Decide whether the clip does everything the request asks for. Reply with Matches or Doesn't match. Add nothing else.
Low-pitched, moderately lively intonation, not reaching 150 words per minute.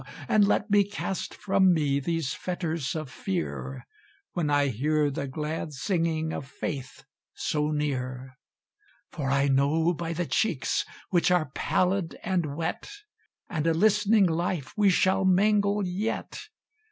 Doesn't match